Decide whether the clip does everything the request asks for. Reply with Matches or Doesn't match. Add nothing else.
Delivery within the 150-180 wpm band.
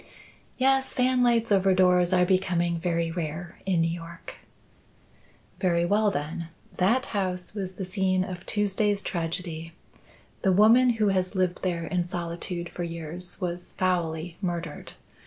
Doesn't match